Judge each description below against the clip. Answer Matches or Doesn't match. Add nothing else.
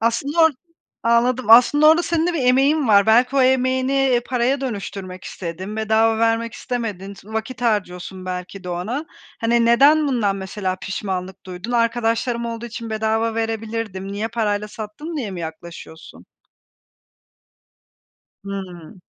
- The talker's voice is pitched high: Matches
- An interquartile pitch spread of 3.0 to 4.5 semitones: Matches